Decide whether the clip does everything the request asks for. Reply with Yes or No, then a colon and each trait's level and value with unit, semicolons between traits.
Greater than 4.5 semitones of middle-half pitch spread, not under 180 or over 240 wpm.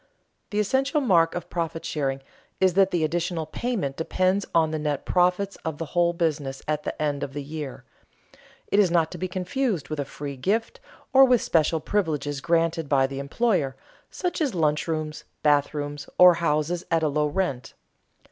No: average, 3.9 semitones; average, 185 wpm